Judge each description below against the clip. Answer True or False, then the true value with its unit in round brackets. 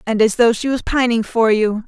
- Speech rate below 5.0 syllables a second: False (5.2 syllables/s)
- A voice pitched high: True (230 Hz)